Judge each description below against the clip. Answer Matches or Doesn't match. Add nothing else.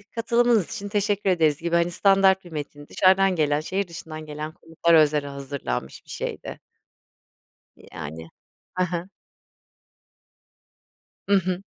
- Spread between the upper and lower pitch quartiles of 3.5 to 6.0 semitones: Matches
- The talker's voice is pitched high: Doesn't match